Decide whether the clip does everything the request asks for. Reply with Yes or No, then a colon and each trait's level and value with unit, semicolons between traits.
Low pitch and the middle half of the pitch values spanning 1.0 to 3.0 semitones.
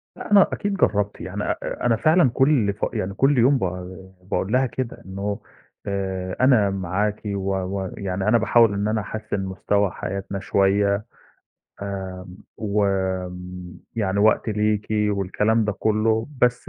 Yes: low, 100 Hz; narrow, 2.5 semitones